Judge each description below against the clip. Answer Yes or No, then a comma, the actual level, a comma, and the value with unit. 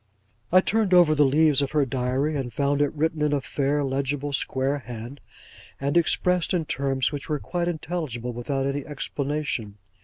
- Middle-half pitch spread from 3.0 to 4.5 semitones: No, narrow, 2.4 semitones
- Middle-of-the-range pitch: Yes, medium, 145 Hz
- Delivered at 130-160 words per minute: No, average, 175 wpm